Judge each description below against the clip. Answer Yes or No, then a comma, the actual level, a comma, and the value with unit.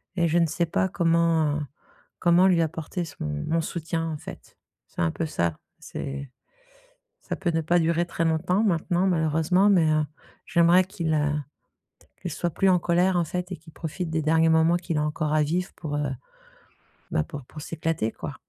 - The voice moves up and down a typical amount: No, narrow, 2.2 semitones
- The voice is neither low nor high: Yes, medium, 165 Hz